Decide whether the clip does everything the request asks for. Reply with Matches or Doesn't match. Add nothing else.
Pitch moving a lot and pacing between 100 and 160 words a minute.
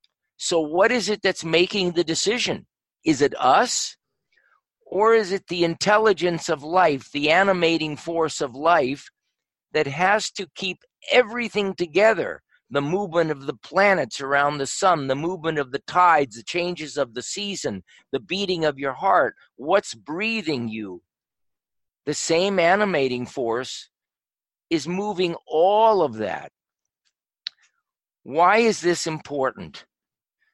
Doesn't match